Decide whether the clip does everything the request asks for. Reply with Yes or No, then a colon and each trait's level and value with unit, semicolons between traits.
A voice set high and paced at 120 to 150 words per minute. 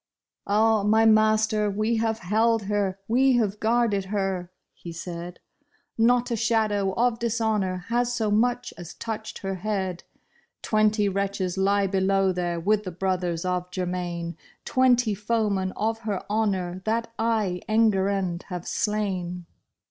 Yes: high, 205 Hz; average, 140 wpm